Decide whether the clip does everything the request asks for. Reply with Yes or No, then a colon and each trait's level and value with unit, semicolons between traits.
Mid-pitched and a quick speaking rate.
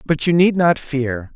Yes: medium, 150 Hz; fast, 220 wpm